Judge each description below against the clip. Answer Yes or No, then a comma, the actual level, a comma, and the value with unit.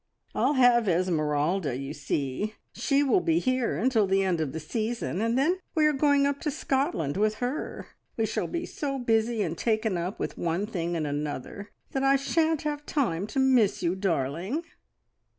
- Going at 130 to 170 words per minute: No, average, 185 wpm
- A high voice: Yes, high, 220 Hz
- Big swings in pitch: Yes, wide, 8.1 semitones